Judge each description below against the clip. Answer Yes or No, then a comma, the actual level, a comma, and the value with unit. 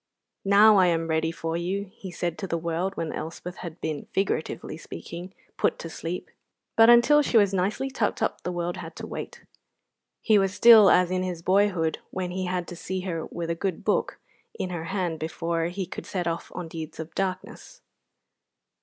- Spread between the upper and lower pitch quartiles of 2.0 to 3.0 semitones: Yes, average, 2.7 semitones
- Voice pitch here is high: No, medium, 180 Hz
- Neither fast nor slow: Yes, average, 195 wpm